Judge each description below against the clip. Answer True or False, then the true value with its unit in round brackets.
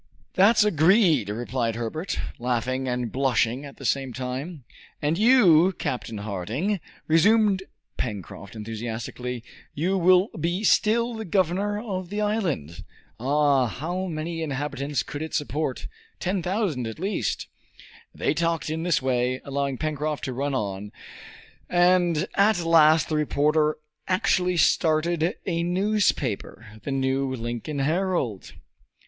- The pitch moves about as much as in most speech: False (6.1 semitones)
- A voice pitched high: False (155 Hz)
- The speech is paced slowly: True (125 wpm)